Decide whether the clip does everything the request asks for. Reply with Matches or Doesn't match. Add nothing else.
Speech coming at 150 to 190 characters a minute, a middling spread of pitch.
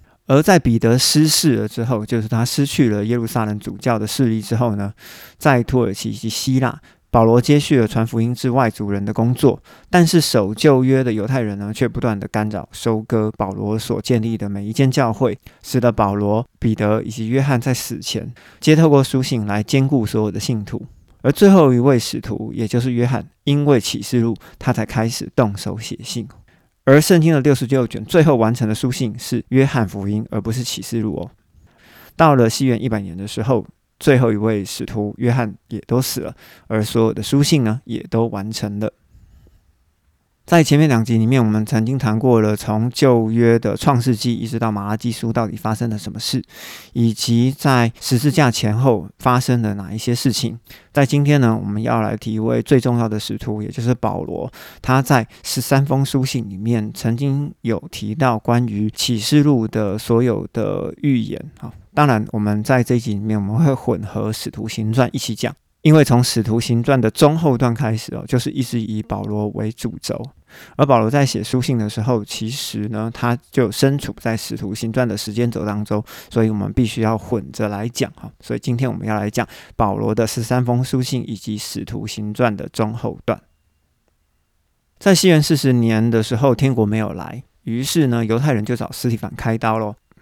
Doesn't match